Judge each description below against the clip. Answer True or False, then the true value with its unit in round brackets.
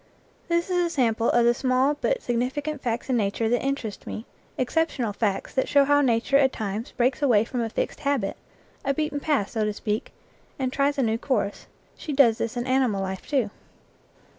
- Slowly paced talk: False (195 wpm)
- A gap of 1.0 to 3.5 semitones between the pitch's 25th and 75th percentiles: False (4.0 semitones)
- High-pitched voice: True (250 Hz)